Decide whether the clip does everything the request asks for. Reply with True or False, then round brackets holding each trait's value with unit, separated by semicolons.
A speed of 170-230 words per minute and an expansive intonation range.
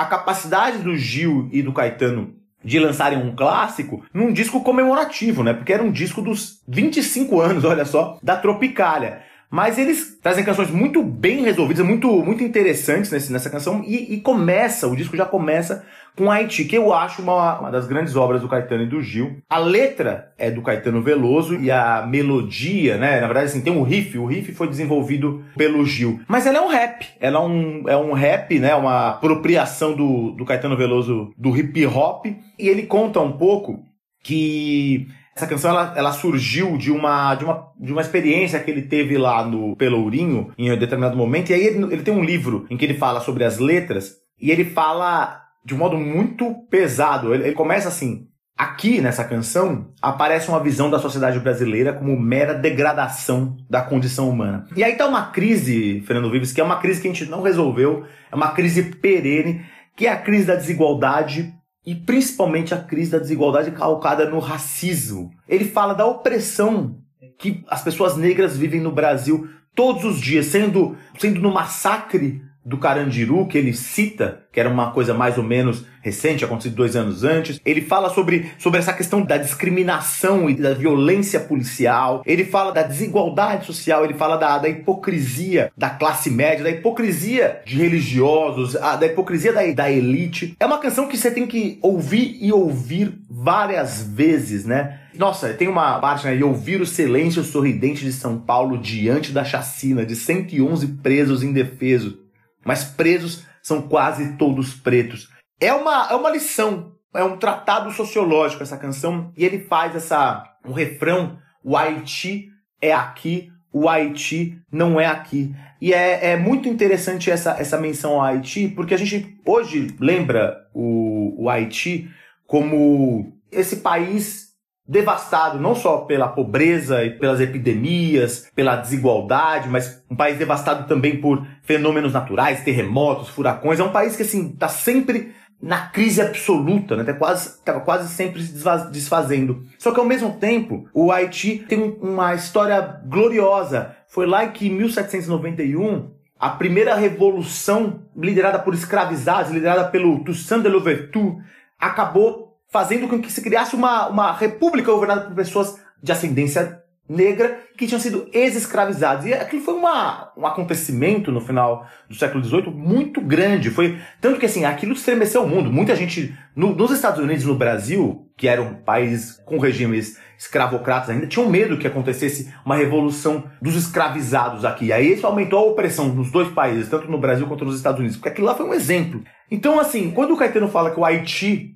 True (175 wpm; 6.0 semitones)